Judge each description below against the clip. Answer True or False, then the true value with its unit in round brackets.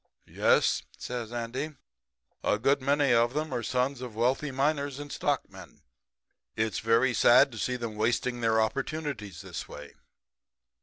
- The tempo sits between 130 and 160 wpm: True (145 wpm)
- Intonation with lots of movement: False (3.4 semitones)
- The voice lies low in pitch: True (125 Hz)